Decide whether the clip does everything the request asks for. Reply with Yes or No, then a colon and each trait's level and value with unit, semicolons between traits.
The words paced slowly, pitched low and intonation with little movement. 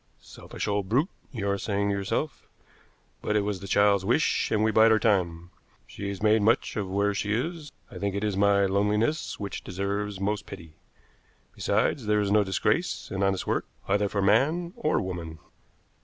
No: average, 185 wpm; low, 100 Hz; narrow, 1.7 semitones